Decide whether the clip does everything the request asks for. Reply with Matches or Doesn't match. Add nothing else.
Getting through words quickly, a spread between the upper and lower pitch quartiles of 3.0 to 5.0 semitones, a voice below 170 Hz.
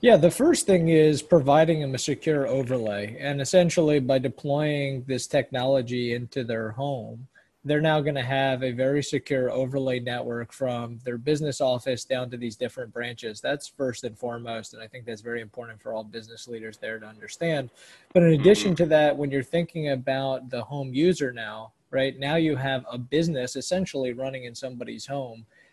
Doesn't match